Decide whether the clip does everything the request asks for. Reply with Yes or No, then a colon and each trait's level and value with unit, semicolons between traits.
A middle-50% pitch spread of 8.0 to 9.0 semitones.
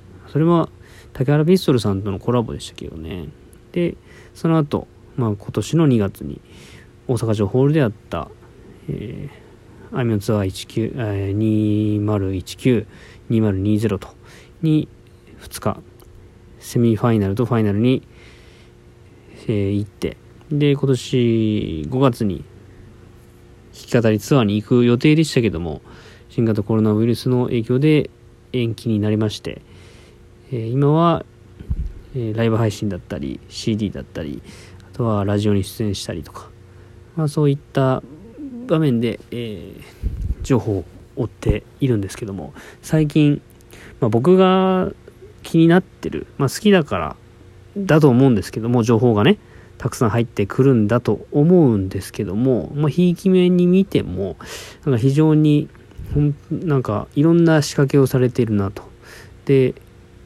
No: average, 5.1 semitones